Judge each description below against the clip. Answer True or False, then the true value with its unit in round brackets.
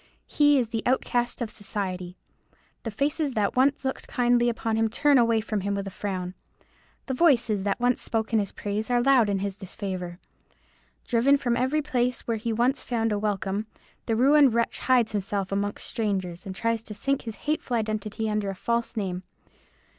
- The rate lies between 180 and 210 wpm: True (185 wpm)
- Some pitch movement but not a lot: True (3.5 semitones)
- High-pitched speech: True (225 Hz)